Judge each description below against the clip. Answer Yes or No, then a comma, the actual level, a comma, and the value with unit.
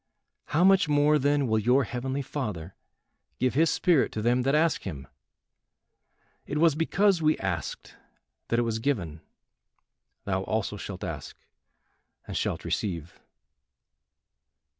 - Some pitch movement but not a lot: No, wide, 6.6 semitones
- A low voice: Yes, low, 130 Hz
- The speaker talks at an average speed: No, slow, 130 wpm